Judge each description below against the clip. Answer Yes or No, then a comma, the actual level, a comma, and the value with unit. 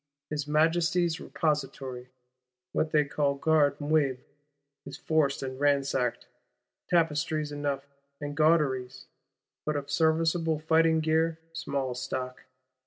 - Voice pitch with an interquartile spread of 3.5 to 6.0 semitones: No, narrow, 2.4 semitones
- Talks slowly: Yes, slow, 105 wpm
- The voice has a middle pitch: Yes, medium, 150 Hz